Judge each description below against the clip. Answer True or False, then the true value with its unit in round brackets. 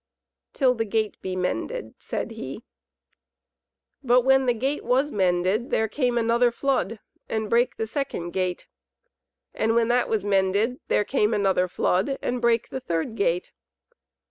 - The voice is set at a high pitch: True (225 Hz)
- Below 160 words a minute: True (150 wpm)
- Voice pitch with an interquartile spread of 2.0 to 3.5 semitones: False (4.2 semitones)